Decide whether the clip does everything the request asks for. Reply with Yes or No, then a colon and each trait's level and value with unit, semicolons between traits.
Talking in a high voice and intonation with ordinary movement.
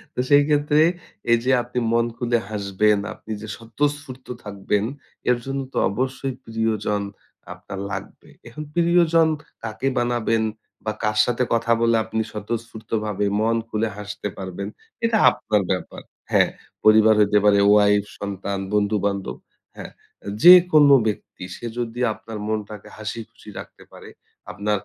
No: low, 110 Hz; average, 3.0 semitones